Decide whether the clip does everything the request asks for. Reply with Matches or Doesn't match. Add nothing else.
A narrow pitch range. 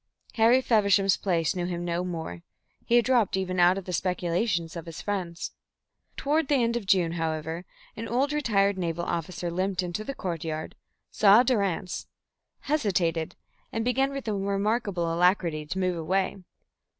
Doesn't match